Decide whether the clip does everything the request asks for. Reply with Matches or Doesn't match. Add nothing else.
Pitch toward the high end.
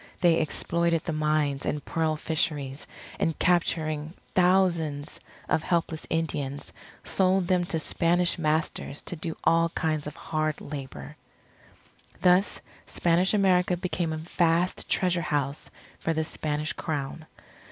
Doesn't match